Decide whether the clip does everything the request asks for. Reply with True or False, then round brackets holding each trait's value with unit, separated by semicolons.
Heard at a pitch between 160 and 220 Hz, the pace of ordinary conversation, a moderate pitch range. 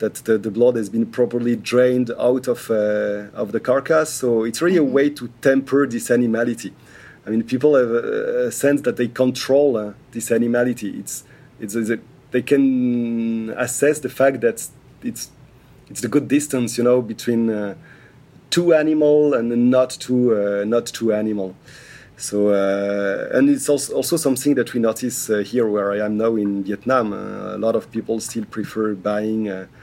False (120 Hz; 185 wpm; 3.6 semitones)